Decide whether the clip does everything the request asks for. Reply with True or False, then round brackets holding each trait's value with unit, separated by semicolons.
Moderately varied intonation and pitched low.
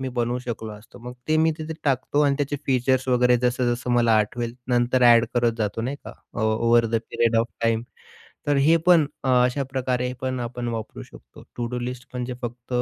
False (1.8 semitones; 125 Hz)